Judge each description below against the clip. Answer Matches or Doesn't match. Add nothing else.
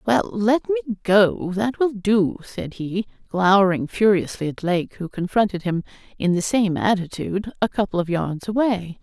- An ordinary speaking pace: Matches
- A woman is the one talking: Matches